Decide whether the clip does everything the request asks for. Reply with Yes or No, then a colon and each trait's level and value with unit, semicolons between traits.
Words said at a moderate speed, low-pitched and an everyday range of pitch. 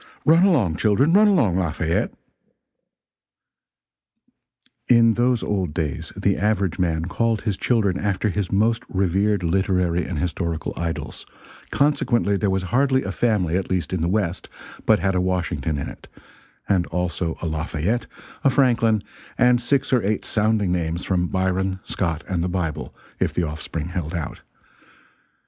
Yes: average, 150 wpm; very low, 95 Hz; average, 4.4 semitones